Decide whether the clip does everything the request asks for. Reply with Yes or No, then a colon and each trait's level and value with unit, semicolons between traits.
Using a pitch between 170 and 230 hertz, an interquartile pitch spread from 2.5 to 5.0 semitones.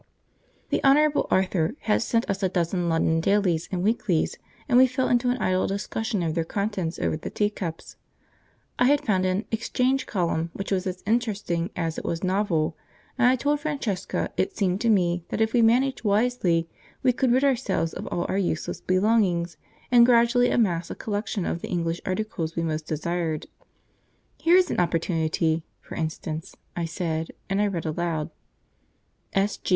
No: high, 190 Hz; wide, 5.6 semitones